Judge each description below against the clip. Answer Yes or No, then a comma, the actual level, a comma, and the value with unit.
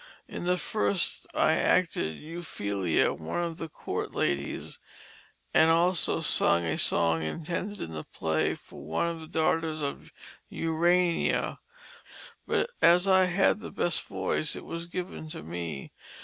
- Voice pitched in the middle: Yes, medium, 160 Hz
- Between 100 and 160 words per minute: Yes, average, 145 wpm